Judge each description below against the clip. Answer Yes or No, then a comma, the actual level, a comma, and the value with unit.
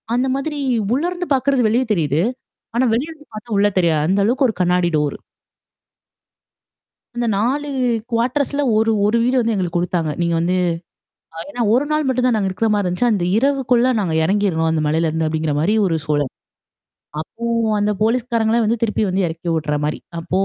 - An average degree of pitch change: No, wide, 6.6 semitones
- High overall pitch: Yes, high, 210 Hz